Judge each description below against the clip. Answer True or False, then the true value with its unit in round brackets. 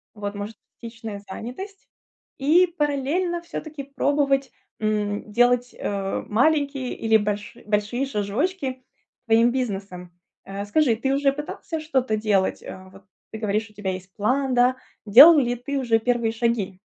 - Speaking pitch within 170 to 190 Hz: False (235 Hz)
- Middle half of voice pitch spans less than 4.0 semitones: False (4.9 semitones)